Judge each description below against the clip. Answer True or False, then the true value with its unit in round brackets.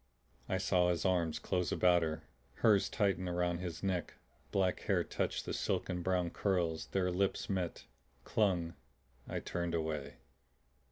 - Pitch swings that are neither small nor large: False (1.8 semitones)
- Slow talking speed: False (145 wpm)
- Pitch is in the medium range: False (90 Hz)